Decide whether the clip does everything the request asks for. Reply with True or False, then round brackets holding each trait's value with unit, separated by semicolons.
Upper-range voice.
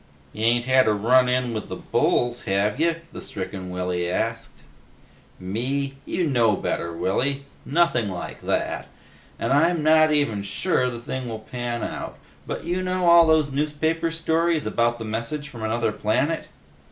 False (125 Hz)